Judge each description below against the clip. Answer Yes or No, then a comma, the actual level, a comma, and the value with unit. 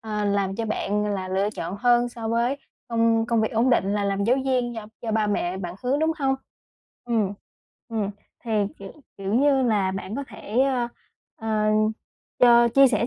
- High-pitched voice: Yes, high, 225 Hz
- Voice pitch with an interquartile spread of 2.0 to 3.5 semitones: Yes, average, 3.2 semitones